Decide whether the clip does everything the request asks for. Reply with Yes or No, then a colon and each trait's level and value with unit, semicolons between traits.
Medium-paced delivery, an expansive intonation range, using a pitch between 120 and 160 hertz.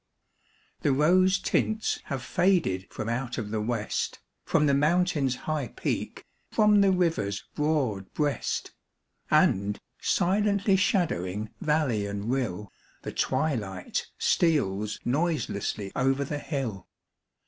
No: slow, 115 wpm; wide, 8.2 semitones; low, 135 Hz